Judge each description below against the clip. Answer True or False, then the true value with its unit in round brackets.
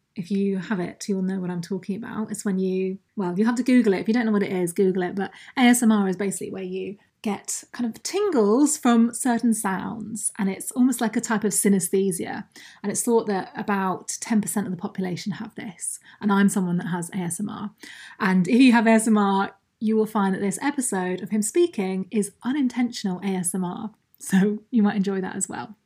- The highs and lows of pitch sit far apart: False (2.9 semitones)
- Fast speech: True (210 wpm)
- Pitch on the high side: True (205 Hz)